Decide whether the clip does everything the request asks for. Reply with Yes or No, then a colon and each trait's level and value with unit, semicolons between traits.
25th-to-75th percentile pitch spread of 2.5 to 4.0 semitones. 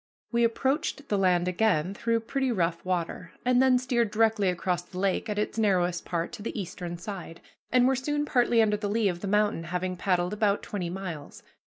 No: average, 4.4 semitones